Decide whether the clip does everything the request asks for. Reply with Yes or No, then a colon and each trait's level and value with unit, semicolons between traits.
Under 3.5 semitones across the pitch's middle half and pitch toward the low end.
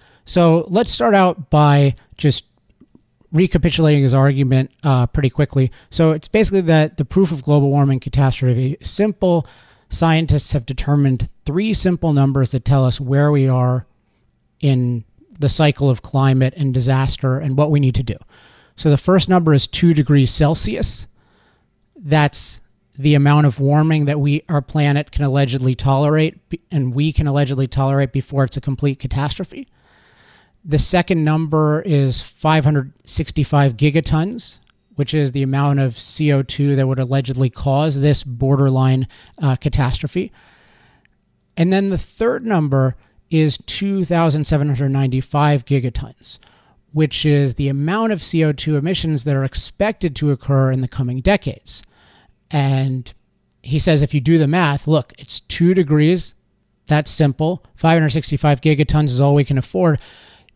No: average, 2.7 semitones; medium, 145 Hz